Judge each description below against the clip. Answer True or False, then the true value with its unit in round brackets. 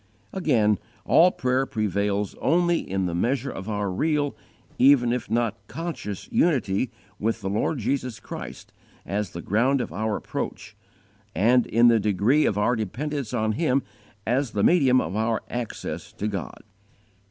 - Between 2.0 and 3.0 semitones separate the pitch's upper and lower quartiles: False (4.6 semitones)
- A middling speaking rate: True (155 wpm)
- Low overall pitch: True (115 Hz)